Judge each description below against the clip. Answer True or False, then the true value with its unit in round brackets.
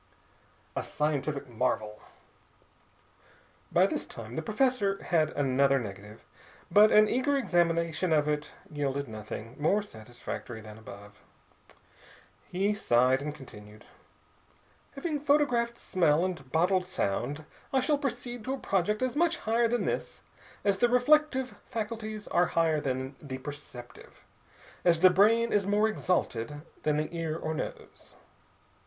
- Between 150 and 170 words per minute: False (135 wpm)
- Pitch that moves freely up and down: True (8.3 semitones)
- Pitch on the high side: False (165 Hz)